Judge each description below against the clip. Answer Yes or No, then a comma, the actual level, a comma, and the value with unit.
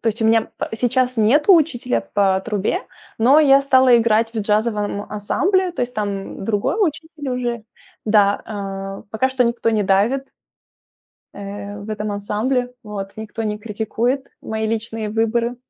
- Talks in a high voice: Yes, high, 225 Hz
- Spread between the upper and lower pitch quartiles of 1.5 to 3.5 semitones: Yes, average, 3.2 semitones